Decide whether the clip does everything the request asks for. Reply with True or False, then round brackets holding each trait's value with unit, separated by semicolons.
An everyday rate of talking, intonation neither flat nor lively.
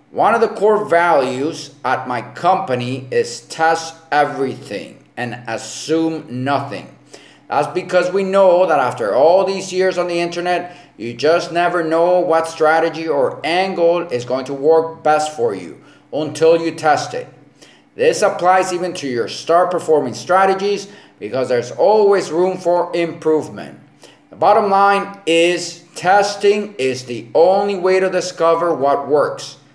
True (145 wpm; 3.7 semitones)